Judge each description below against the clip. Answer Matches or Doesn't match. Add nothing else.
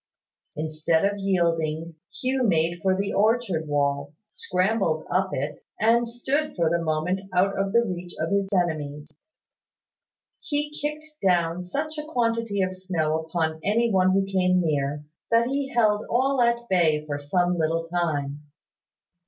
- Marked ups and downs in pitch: Matches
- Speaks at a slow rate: Doesn't match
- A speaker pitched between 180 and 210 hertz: Matches